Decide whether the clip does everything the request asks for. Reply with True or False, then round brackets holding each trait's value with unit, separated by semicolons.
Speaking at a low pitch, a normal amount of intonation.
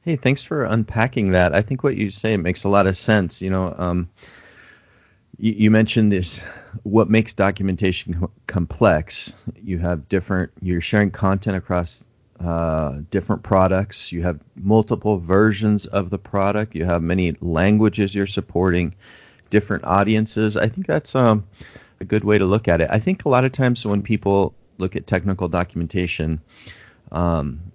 True (100 Hz; 3.3 semitones)